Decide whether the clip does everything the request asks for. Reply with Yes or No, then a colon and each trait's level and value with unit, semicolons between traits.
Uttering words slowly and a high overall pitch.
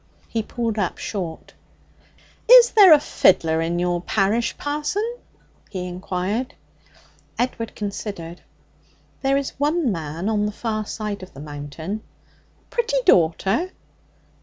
Yes: slow, 120 wpm; high, 210 Hz